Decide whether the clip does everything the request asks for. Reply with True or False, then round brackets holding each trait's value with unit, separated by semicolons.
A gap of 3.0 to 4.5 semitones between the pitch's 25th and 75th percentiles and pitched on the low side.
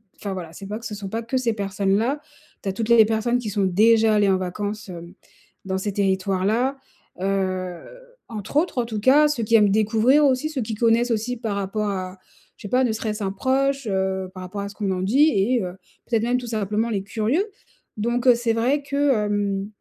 False (3.5 semitones; 215 Hz)